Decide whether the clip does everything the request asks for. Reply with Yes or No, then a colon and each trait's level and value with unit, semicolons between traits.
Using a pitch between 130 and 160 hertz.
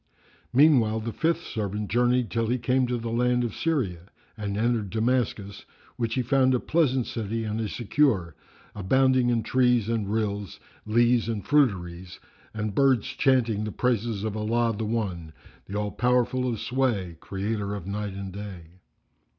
No: low, 115 Hz